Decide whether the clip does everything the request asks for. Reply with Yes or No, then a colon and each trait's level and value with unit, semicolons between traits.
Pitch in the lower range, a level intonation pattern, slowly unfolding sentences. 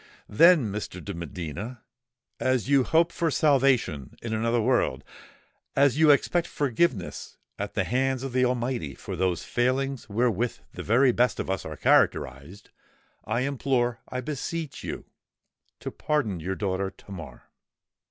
No: low, 120 Hz; average, 5.3 semitones; slow, 130 wpm